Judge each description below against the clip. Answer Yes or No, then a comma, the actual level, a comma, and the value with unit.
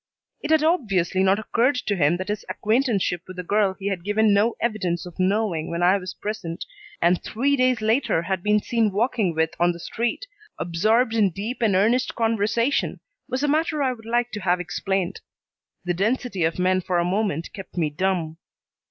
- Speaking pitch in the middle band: No, high, 200 Hz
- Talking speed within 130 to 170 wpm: No, average, 195 wpm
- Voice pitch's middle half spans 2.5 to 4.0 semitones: No, average, 4.5 semitones